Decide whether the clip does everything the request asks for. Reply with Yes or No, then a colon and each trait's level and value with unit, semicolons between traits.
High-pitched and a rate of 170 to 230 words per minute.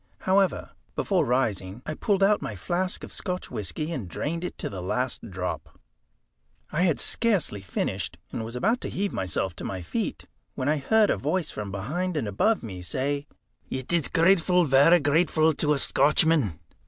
No: medium, 145 Hz; average, 180 wpm